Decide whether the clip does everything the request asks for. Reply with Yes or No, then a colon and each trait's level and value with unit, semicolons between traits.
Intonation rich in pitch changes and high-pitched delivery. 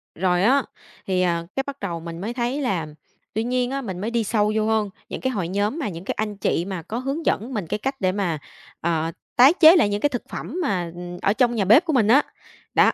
Yes: wide, 5.7 semitones; high, 210 Hz